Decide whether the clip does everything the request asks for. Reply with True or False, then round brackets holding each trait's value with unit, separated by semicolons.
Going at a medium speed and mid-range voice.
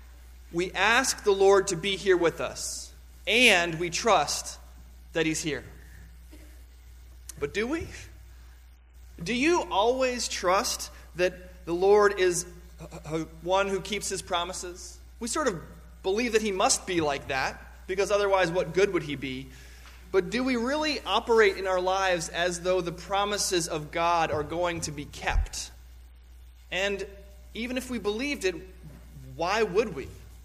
True (150 wpm; 175 Hz)